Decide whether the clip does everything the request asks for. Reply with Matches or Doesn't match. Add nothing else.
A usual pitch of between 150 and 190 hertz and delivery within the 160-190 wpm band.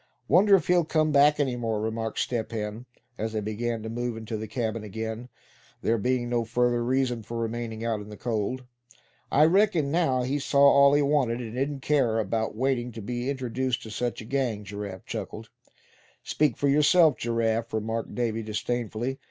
Doesn't match